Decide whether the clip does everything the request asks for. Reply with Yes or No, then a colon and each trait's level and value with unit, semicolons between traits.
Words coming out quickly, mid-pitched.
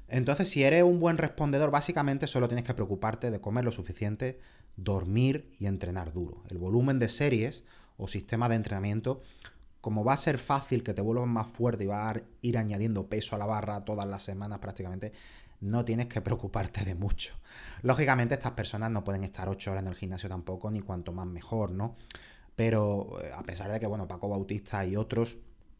No: fast, 195 wpm; low, 110 Hz